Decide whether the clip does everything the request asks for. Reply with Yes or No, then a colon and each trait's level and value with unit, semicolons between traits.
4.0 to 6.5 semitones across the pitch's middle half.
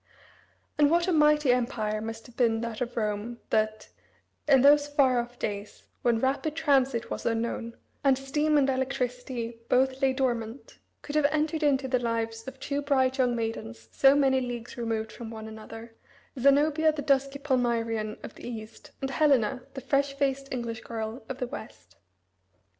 No: average, 3.3 semitones